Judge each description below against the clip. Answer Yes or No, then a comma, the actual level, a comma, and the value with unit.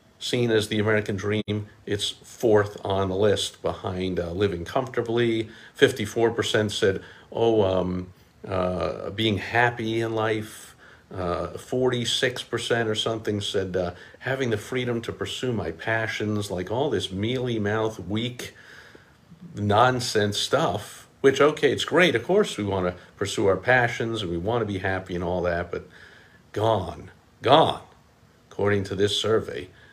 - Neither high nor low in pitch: No, low, 105 Hz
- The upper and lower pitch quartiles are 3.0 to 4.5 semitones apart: Yes, average, 3.3 semitones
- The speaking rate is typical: Yes, average, 145 wpm